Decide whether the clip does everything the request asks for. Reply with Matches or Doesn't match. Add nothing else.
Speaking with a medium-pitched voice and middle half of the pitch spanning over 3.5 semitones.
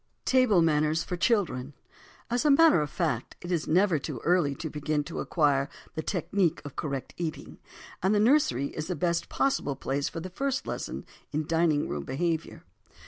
Matches